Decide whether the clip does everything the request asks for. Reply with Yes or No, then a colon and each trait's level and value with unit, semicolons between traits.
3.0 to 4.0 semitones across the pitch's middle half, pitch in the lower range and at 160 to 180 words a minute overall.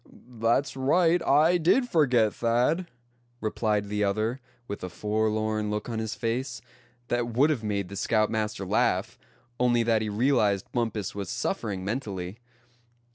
No: average, 3.3 semitones; low, 115 Hz; average, 140 wpm